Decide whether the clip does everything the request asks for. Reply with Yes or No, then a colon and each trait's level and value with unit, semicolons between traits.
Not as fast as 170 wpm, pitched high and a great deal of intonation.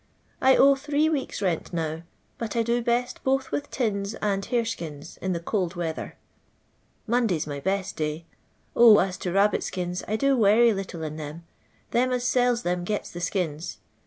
No: average, 190 wpm; high, 200 Hz; wide, 5.7 semitones